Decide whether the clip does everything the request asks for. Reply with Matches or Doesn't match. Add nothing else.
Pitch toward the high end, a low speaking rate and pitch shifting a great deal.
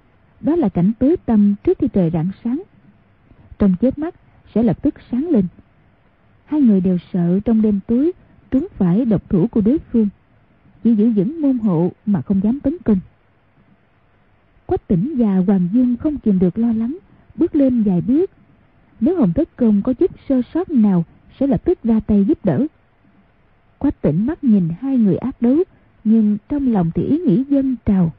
Doesn't match